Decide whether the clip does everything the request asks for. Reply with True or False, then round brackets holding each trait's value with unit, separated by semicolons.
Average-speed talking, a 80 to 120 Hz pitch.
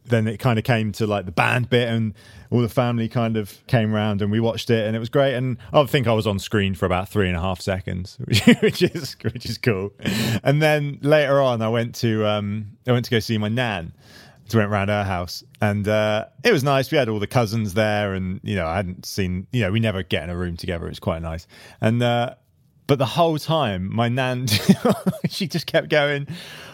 False (240 wpm; 115 Hz)